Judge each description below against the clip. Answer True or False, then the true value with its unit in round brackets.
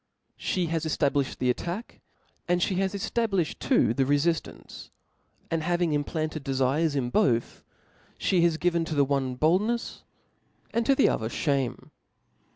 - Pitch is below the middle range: False (160 Hz)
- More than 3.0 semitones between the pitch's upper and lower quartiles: True (4.2 semitones)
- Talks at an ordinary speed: True (145 wpm)